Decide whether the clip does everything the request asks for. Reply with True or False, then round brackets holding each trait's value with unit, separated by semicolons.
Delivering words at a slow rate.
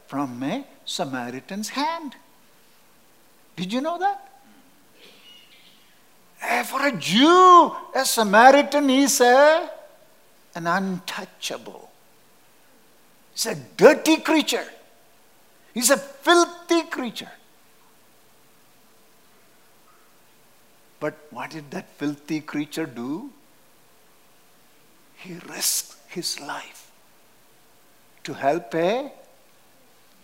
True (75 wpm)